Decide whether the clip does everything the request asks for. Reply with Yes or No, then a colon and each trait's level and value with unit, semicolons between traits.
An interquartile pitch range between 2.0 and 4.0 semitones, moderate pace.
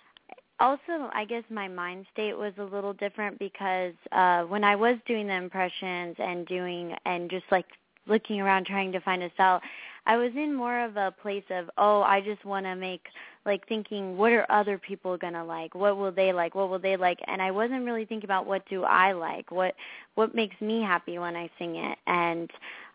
No: narrow, 2.6 semitones; fast, 210 wpm